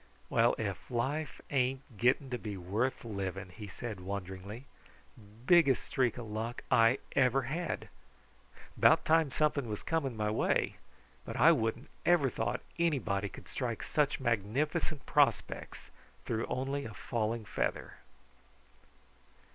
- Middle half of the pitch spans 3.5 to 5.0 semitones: Yes, average, 4.4 semitones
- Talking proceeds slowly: Yes, slow, 130 wpm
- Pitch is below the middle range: Yes, low, 120 Hz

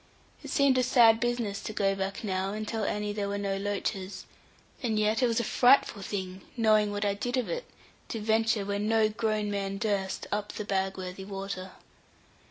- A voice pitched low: No, high, 210 Hz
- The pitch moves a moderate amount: No, narrow, 2.2 semitones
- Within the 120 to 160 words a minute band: No, average, 190 wpm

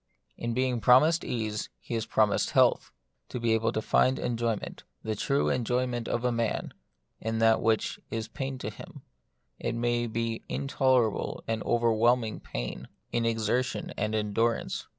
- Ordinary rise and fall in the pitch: No, narrow, 1.9 semitones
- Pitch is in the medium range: No, low, 115 Hz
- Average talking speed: Yes, average, 165 wpm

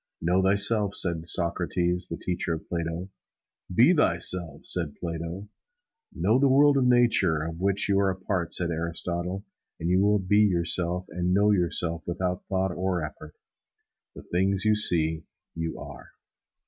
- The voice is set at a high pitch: No, very low, 90 Hz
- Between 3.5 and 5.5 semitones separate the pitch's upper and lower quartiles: No, average, 2.7 semitones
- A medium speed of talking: Yes, average, 155 wpm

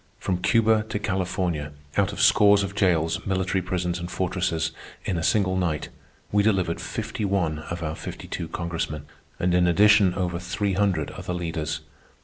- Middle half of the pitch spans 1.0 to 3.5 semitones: Yes, average, 2.7 semitones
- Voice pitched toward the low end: Yes, very low, 90 Hz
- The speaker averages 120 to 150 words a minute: No, average, 165 wpm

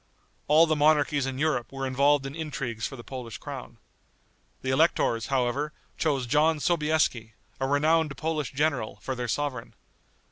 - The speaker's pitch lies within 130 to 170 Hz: Yes, medium, 140 Hz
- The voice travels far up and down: No, average, 3.1 semitones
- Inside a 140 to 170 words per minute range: Yes, average, 150 wpm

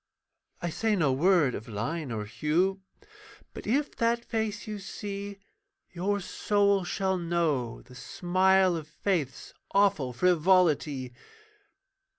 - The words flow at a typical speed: No, slow, 120 wpm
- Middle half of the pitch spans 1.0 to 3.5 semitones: No, average, 5.1 semitones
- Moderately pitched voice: Yes, medium, 180 Hz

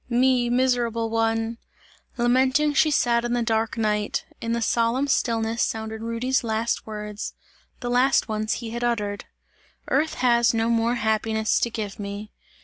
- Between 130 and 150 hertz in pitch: No, high, 230 Hz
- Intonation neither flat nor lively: No, narrow, 1.7 semitones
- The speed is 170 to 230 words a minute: No, average, 150 wpm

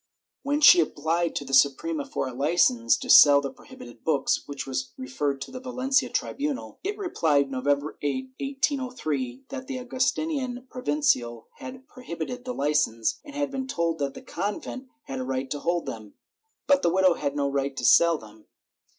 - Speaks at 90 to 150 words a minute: No, average, 175 wpm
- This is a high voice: No, medium, 165 Hz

